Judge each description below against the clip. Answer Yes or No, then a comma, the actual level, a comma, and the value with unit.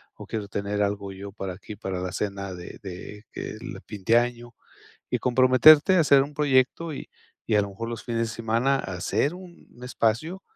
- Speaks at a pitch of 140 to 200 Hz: No, low, 115 Hz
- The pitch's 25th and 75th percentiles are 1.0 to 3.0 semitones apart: No, average, 4.6 semitones